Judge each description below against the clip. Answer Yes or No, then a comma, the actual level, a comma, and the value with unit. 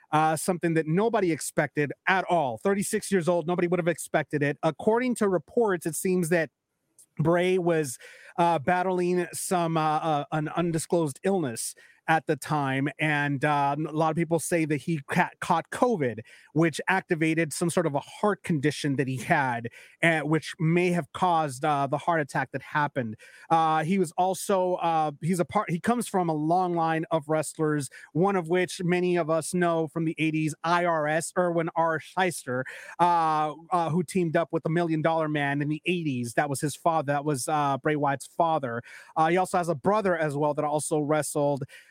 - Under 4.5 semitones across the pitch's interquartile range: Yes, average, 2.7 semitones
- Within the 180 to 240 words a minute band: Yes, average, 190 wpm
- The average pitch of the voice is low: No, medium, 165 Hz